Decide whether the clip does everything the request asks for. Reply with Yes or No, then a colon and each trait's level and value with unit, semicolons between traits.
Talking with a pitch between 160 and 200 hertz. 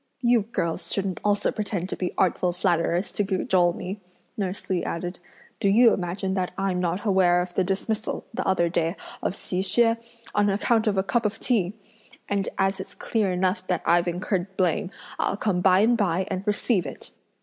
Yes: high, 190 Hz